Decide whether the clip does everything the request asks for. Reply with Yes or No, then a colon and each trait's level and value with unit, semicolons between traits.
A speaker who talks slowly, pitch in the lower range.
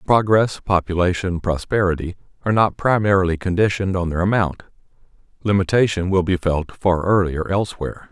Yes: slow, 125 wpm; very low, 95 Hz